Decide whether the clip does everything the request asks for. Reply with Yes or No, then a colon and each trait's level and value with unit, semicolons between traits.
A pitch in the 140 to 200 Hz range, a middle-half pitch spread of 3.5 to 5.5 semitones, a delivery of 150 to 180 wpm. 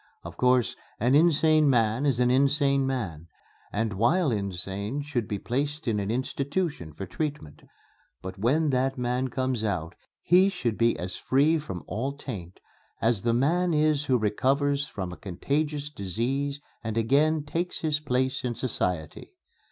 No: low, 130 Hz; average, 5.2 semitones; average, 155 wpm